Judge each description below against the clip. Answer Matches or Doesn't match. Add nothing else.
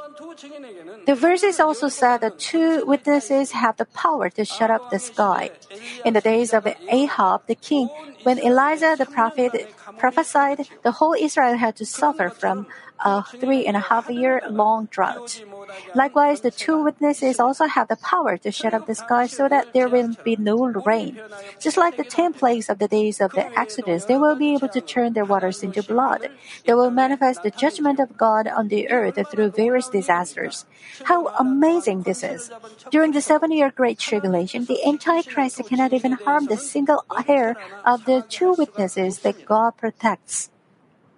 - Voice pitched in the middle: Doesn't match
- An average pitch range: Matches